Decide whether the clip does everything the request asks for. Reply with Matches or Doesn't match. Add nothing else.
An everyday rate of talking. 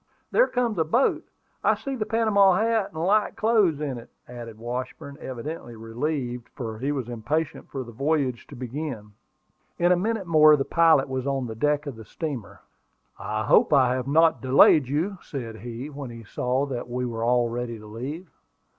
Matches